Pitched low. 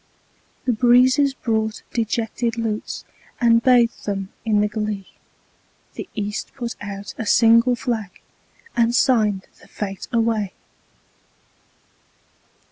No: high, 225 Hz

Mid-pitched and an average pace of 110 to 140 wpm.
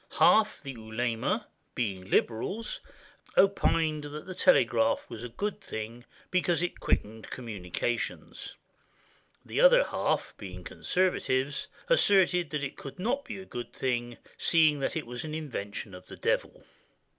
Yes: medium, 150 Hz; slow, 135 wpm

